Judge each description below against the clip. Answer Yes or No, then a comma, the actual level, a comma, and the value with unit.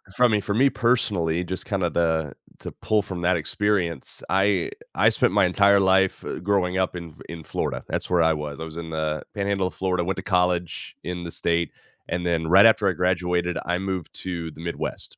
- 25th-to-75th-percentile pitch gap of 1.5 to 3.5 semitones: Yes, narrow, 2.4 semitones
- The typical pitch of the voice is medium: No, very low, 90 Hz